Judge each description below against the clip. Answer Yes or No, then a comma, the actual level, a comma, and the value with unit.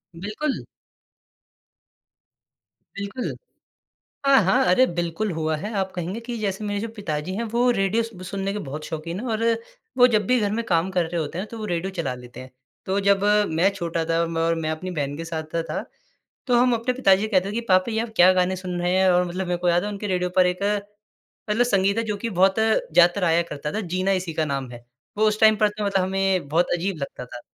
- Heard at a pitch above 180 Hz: Yes, high, 190 Hz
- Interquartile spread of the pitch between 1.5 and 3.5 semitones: No, average, 3.9 semitones